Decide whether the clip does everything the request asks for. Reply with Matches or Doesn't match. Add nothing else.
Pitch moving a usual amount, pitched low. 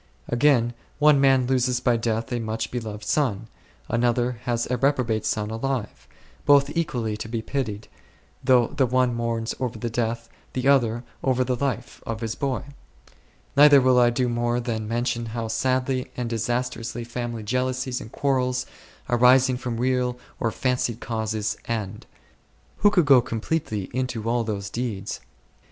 Doesn't match